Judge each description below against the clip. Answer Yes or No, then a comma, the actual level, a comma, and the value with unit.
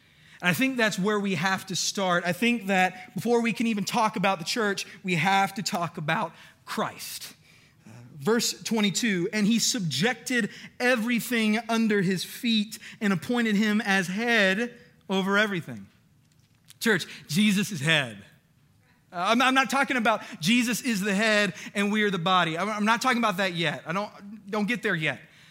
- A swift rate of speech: No, average, 175 wpm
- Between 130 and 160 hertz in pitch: No, high, 205 Hz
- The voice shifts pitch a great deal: No, average, 3.9 semitones